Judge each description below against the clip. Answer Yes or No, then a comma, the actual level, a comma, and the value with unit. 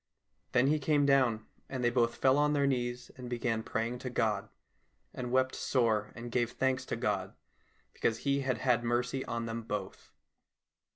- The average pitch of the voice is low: Yes, low, 120 Hz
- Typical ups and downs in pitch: No, narrow, 2.2 semitones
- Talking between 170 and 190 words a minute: Yes, average, 175 wpm